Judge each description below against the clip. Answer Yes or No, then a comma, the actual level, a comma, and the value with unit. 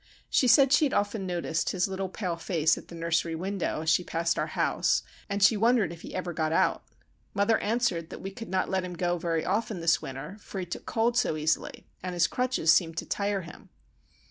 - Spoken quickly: Yes, fast, 220 wpm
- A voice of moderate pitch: Yes, medium, 180 Hz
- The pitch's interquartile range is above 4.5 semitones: No, average, 3.5 semitones